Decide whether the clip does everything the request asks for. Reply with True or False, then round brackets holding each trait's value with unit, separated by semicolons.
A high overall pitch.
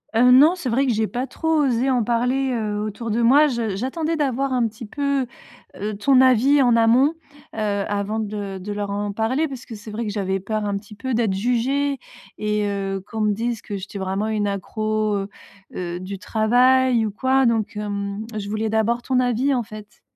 True (220 Hz)